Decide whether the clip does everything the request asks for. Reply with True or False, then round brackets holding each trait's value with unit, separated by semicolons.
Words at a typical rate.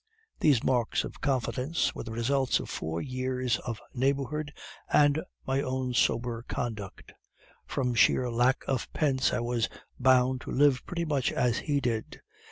True (155 wpm)